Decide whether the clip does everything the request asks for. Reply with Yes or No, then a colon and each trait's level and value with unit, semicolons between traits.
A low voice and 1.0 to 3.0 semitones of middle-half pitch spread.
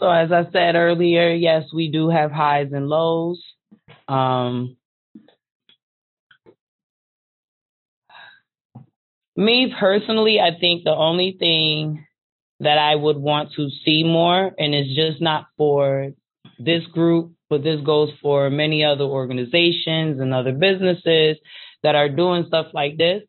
No: medium, 160 Hz; narrow, 2.5 semitones